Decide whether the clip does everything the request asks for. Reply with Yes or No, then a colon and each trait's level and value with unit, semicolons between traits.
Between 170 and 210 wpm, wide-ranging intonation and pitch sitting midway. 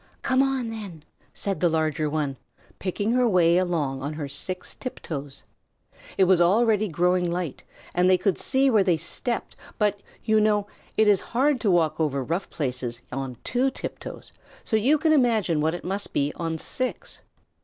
Yes: average, 175 wpm; wide, 5.7 semitones; medium, 180 Hz